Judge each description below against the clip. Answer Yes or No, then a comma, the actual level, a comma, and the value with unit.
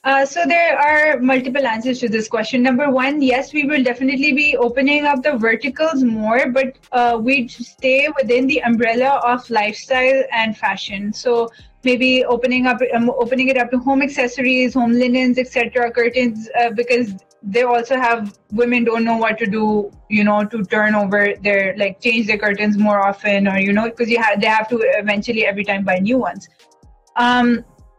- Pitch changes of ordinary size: Yes, average, 3.1 semitones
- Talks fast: No, average, 185 wpm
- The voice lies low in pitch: No, high, 240 Hz